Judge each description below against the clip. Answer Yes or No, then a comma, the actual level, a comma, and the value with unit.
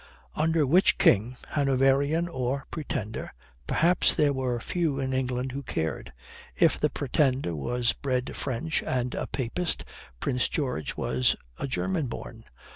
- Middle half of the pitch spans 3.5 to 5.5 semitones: No, average, 3.1 semitones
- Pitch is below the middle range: Yes, low, 130 Hz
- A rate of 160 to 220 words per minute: No, slow, 135 wpm